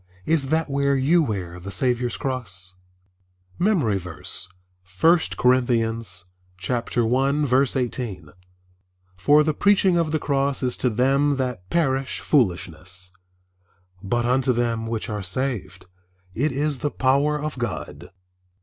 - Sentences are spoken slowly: Yes, slow, 120 wpm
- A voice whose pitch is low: Yes, low, 125 Hz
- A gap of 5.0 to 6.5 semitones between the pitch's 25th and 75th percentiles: Yes, wide, 5.4 semitones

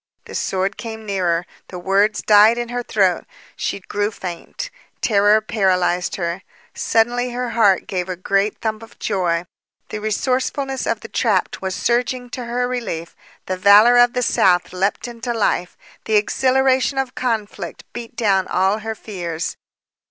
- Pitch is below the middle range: No, high, 215 Hz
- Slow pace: No, average, 155 wpm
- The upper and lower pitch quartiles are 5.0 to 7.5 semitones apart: No, average, 4.2 semitones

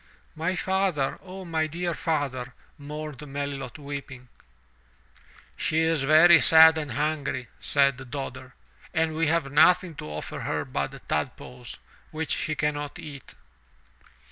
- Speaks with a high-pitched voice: No, medium, 150 Hz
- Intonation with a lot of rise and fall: No, average, 2.9 semitones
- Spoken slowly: Yes, slow, 125 wpm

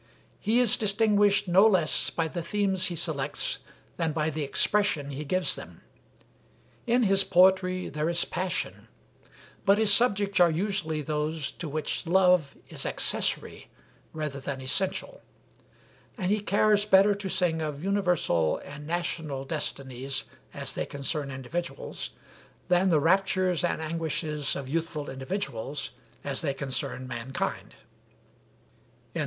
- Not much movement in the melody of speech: No, average, 4.8 semitones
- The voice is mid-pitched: Yes, medium, 170 Hz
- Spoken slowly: Yes, slow, 130 wpm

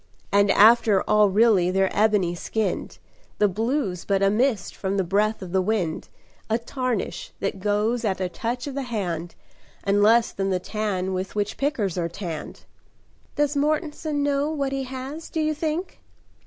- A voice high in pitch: Yes, high, 210 Hz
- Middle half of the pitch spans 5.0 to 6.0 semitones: Yes, wide, 5.5 semitones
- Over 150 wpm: Yes, average, 170 wpm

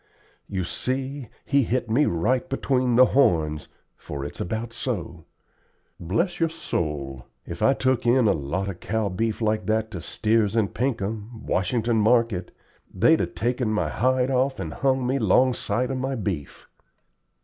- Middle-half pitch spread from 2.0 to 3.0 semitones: No, average, 5.0 semitones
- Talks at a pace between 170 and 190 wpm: No, average, 160 wpm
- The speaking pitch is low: Yes, low, 115 Hz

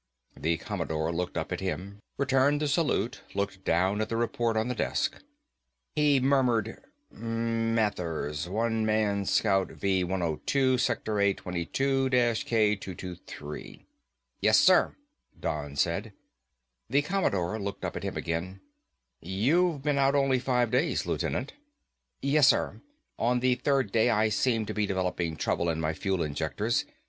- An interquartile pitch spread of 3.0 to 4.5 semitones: No, wide, 5.6 semitones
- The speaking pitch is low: Yes, low, 110 Hz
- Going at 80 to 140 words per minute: Yes, slow, 135 wpm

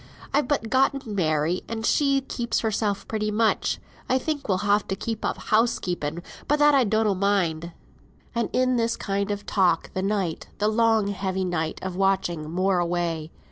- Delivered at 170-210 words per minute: Yes, average, 180 wpm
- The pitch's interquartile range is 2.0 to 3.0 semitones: No, average, 4.1 semitones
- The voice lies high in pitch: Yes, high, 205 Hz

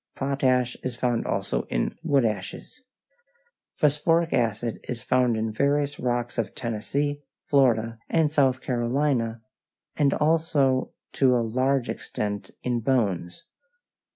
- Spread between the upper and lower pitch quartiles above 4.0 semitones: No, average, 3.6 semitones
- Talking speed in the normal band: No, slow, 125 wpm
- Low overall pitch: Yes, low, 125 Hz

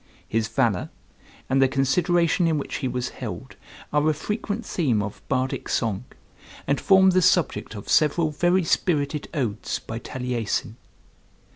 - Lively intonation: Yes, wide, 5.9 semitones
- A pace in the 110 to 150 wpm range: Yes, average, 145 wpm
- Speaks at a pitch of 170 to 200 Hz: No, medium, 140 Hz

